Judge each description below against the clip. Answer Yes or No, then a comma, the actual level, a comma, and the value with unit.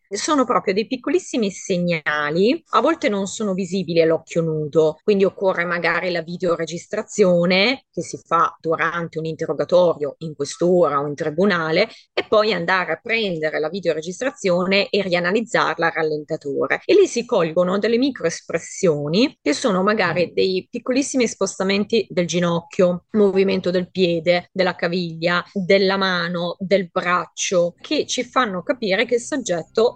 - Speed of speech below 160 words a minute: Yes, average, 140 wpm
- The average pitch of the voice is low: No, medium, 180 Hz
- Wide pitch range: No, average, 4.0 semitones